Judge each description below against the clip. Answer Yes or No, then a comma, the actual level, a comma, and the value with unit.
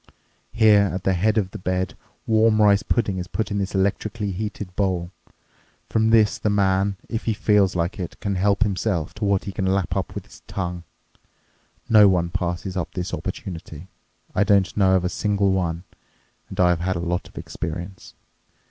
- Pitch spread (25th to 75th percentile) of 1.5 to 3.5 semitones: Yes, narrow, 2.5 semitones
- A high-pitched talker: No, very low, 95 Hz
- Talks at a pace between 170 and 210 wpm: Yes, average, 190 wpm